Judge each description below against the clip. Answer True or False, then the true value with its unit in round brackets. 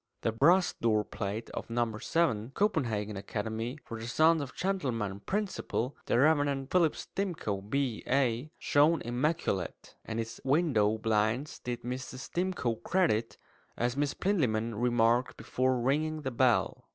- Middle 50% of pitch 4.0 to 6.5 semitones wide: True (5.3 semitones)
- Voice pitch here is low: True (125 Hz)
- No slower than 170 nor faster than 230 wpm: False (135 wpm)